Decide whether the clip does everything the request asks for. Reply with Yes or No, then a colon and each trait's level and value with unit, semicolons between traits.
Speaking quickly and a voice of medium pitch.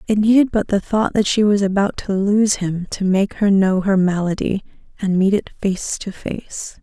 No: fast, 210 wpm; high, 200 Hz